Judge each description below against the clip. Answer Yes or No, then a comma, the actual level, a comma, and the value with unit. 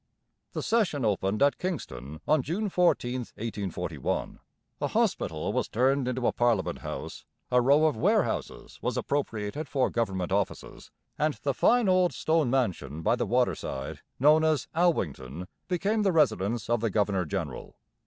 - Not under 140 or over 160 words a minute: Yes, average, 150 wpm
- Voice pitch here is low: Yes, low, 125 Hz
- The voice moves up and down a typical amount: No, wide, 7.3 semitones